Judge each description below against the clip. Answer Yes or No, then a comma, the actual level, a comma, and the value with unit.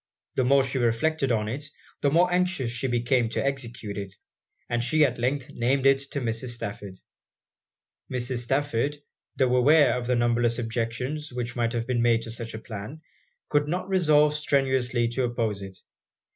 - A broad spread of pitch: No, average, 3.1 semitones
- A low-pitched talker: Yes, low, 125 Hz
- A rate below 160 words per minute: No, average, 170 wpm